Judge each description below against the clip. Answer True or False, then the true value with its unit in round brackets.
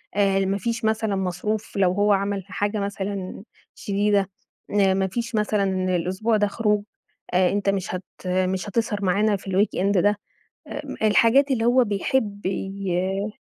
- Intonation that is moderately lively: False (1.8 semitones)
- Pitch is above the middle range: True (200 Hz)